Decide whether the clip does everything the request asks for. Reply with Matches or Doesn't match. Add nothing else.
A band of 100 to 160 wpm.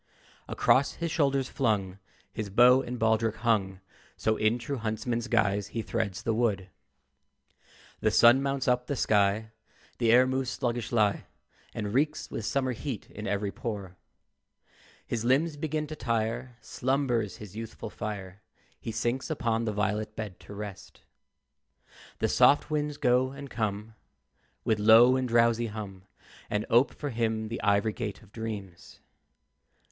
Matches